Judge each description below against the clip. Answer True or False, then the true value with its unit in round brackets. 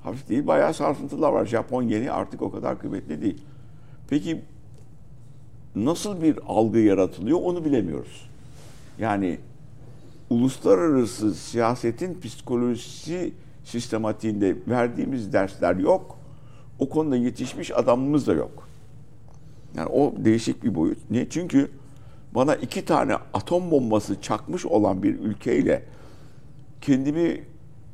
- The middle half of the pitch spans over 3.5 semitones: False (2.9 semitones)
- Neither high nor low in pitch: False (130 Hz)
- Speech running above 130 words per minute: False (105 wpm)